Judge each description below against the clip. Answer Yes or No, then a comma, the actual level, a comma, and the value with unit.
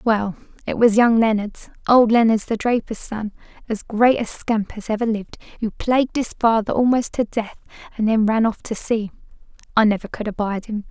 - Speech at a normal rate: Yes, average, 185 wpm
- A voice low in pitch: No, high, 220 Hz